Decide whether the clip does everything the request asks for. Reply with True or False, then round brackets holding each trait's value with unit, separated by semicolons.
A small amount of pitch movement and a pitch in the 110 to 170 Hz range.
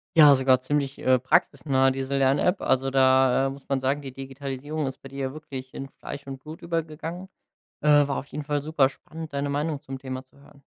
True (1.9 semitones; 140 Hz)